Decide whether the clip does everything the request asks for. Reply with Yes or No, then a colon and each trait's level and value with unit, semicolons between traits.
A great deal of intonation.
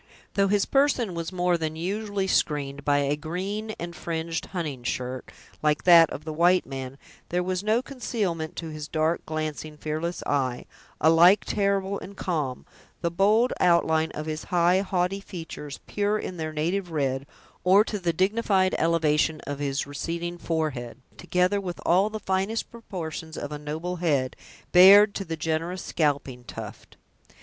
No: average, 3.8 semitones